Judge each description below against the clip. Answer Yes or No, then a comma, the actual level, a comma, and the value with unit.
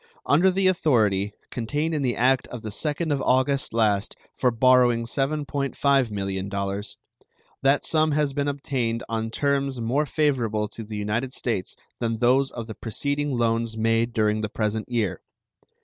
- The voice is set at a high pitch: No, low, 120 Hz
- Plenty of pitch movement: No, average, 4.1 semitones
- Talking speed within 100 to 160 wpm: Yes, average, 155 wpm